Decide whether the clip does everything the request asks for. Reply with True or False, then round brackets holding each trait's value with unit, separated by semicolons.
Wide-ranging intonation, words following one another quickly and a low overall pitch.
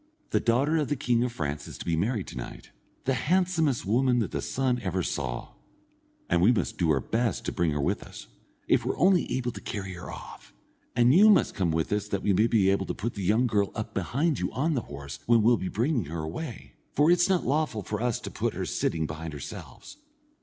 True (6.6 semitones; 235 wpm; 115 Hz)